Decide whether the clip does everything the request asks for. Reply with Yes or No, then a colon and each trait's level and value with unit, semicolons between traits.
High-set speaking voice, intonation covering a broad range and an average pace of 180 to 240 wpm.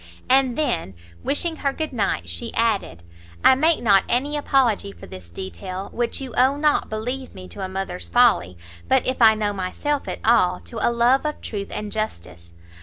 Yes: high, 220 Hz; wide, 6.6 semitones; average, 185 wpm